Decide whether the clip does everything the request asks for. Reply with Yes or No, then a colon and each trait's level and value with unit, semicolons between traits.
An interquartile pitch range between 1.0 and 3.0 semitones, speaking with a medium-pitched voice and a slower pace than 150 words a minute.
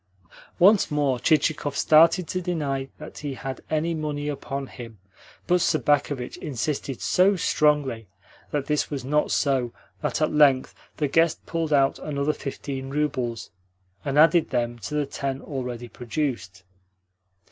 Yes: narrow, 2.5 semitones; medium, 145 Hz; average, 140 wpm